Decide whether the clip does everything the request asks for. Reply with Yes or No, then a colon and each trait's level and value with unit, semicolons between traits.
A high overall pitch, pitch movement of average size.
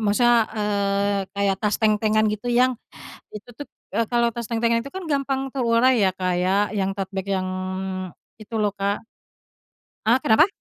Yes: high, 215 Hz; average, 3.1 semitones